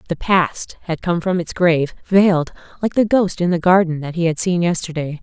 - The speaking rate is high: Yes, fast, 220 wpm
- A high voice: No, medium, 175 Hz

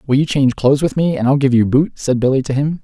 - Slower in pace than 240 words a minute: No, fast, 315 wpm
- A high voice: No, low, 135 Hz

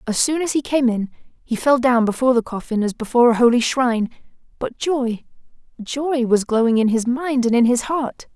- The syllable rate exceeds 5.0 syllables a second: Yes, 5.4 syllables/s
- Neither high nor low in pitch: No, high, 245 Hz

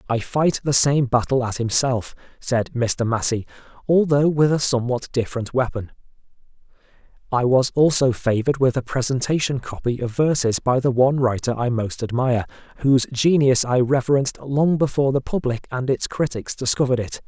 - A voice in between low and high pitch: No, low, 130 Hz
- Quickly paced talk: No, average, 160 wpm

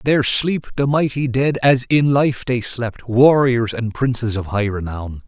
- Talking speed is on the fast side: No, average, 180 wpm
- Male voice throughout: Yes, male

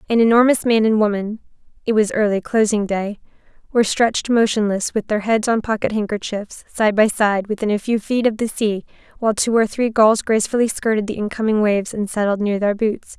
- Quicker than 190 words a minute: Yes, average, 200 wpm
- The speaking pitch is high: Yes, high, 215 Hz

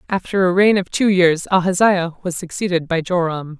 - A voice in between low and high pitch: Yes, medium, 180 Hz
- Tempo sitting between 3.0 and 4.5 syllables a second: No, 5.2 syllables/s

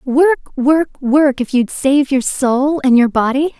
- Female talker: Yes, female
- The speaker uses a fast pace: No, average, 185 wpm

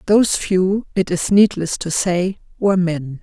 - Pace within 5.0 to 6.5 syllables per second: No, 4.3 syllables/s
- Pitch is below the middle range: No, medium, 185 Hz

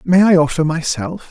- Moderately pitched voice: Yes, medium, 165 Hz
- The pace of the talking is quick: No, average, 185 wpm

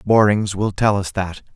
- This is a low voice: Yes, low, 100 Hz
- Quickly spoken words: No, average, 190 wpm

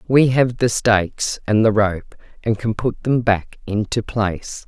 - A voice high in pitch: No, low, 110 Hz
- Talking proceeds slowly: No, average, 180 wpm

